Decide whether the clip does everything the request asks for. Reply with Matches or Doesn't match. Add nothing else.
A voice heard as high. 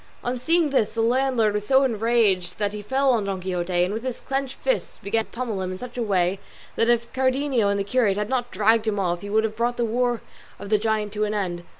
Matches